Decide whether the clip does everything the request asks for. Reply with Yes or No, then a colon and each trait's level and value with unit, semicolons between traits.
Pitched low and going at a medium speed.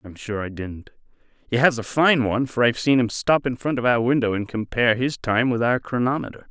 No: low, 120 Hz; fast, 240 wpm